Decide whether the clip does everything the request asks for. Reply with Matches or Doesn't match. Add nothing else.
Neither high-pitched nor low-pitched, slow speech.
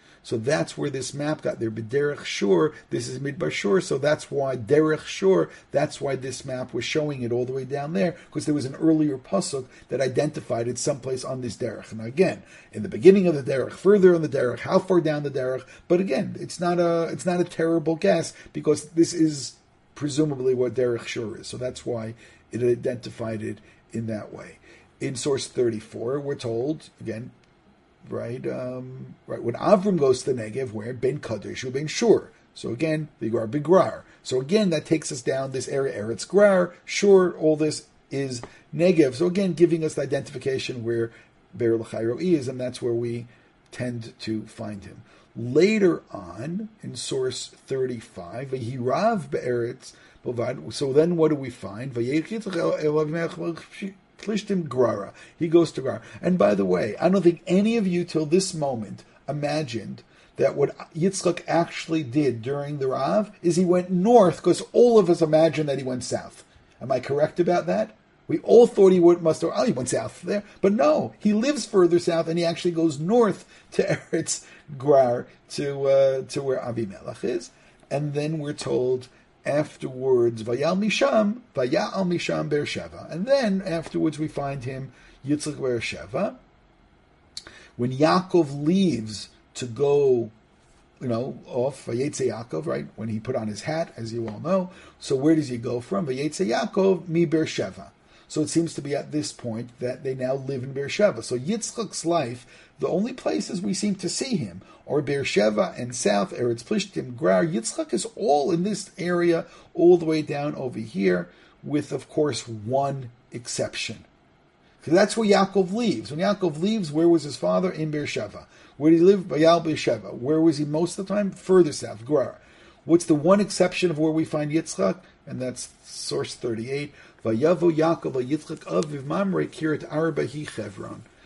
Doesn't match